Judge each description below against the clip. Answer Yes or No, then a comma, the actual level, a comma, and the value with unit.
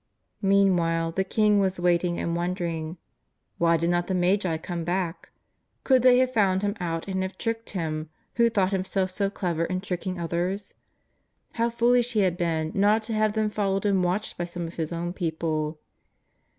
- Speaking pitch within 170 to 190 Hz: Yes, medium, 185 Hz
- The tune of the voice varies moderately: Yes, average, 3.1 semitones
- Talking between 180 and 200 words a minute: Yes, average, 185 wpm